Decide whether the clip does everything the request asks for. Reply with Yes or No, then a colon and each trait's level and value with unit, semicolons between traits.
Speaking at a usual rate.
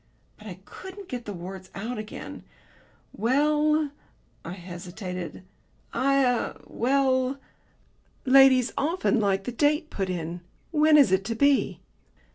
No: slow, 125 wpm